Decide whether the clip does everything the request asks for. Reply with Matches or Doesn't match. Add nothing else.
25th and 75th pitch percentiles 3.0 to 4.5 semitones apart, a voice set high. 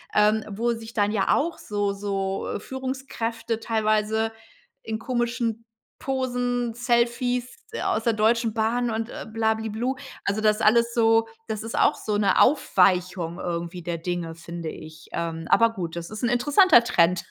Matches